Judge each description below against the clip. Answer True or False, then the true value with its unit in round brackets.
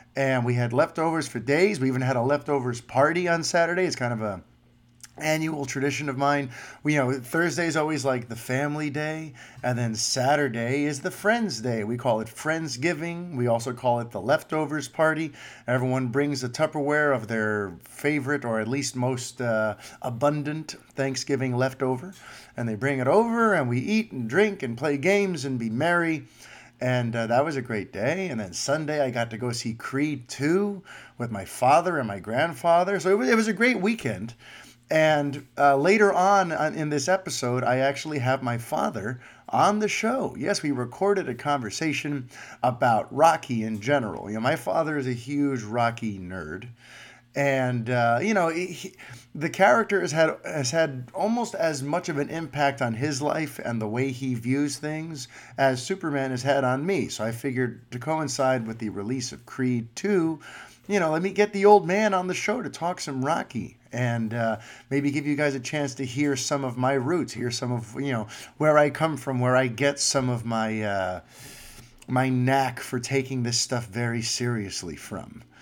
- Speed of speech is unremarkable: True (195 wpm)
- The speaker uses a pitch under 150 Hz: True (135 Hz)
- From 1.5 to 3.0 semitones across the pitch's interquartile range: False (4.4 semitones)